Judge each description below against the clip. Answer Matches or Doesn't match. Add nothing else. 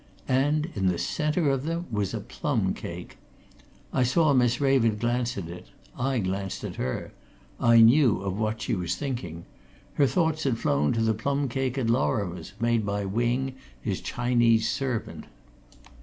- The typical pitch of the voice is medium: Doesn't match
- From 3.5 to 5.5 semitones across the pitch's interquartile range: Matches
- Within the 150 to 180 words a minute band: Matches